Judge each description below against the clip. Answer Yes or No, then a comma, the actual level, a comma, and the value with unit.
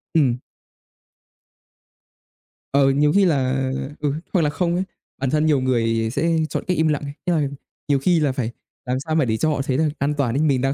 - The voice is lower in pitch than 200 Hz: Yes, medium, 140 Hz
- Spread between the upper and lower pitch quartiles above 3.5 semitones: No, average, 3.2 semitones